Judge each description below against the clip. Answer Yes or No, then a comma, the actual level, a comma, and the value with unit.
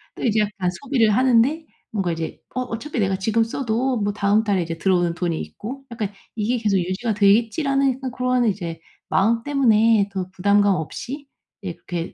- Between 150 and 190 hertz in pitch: No, high, 215 Hz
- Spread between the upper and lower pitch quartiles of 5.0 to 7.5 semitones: No, average, 4.5 semitones